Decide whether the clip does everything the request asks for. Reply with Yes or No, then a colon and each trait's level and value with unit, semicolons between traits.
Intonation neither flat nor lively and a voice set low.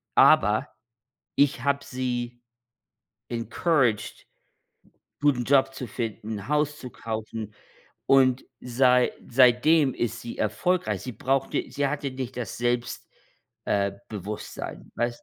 Yes: average, 3.0 semitones; low, 125 Hz